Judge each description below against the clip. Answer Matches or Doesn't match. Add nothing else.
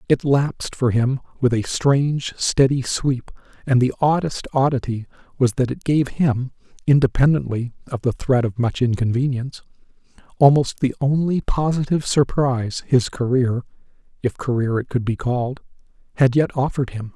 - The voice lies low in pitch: Matches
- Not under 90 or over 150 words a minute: Matches